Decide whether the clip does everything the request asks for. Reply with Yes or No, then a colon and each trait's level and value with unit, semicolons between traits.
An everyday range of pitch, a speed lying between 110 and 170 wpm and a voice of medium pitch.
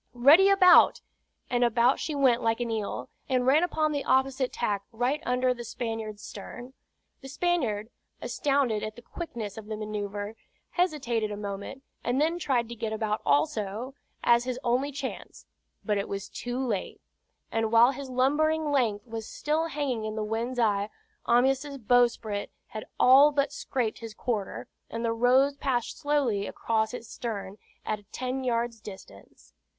No: average, 3.8 semitones; average, 160 wpm; high, 240 Hz